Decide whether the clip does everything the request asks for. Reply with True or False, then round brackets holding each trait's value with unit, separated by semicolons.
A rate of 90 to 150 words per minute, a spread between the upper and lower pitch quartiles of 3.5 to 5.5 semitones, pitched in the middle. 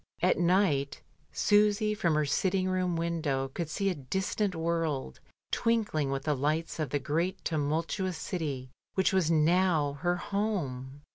True (145 wpm; 4.6 semitones; 165 Hz)